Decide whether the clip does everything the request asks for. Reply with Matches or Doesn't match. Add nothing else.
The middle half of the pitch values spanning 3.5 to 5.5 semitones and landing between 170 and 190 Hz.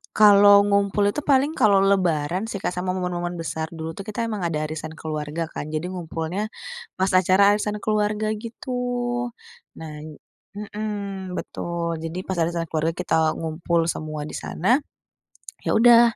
Matches